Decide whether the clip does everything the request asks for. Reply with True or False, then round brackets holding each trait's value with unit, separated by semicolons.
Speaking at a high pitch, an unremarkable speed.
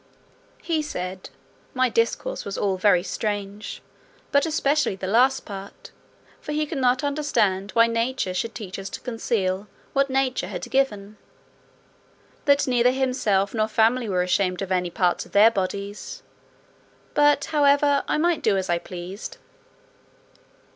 True (225 Hz; 145 wpm)